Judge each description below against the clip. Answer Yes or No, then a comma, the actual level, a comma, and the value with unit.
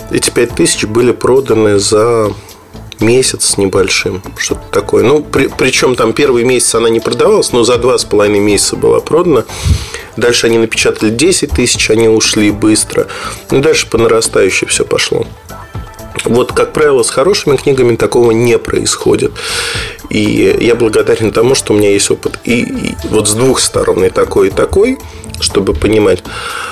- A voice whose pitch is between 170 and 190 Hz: No, low, 125 Hz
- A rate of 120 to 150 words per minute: No, fast, 160 wpm